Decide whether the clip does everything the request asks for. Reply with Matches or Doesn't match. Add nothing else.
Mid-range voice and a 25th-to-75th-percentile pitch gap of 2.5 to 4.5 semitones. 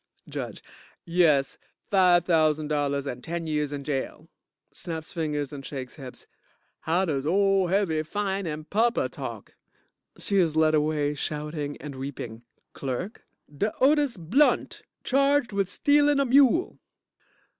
Doesn't match